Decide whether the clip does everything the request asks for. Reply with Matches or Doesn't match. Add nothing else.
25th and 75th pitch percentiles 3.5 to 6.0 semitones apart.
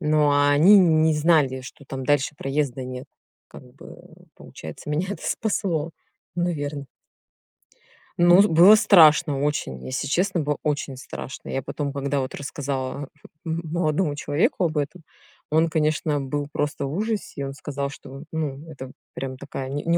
Doesn't match